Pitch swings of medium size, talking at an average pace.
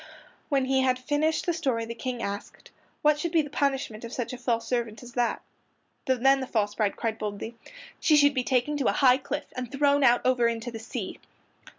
No: average, 3.4 semitones; fast, 210 wpm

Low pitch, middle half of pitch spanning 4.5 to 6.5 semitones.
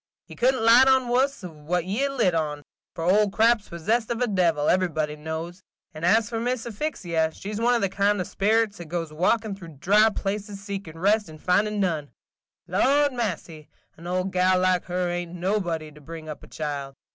No: medium, 185 Hz; average, 5.0 semitones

